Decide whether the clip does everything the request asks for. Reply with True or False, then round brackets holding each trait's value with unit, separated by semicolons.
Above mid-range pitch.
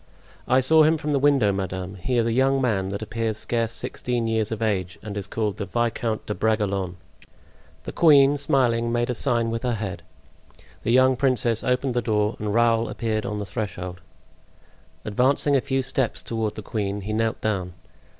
False (115 Hz)